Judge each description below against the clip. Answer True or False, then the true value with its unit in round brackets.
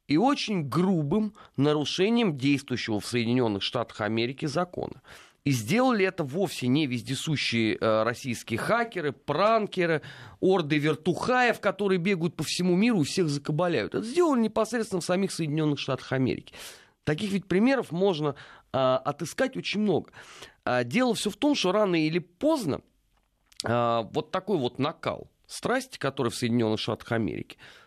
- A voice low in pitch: False (160 Hz)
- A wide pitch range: True (7.5 semitones)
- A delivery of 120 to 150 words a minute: True (135 wpm)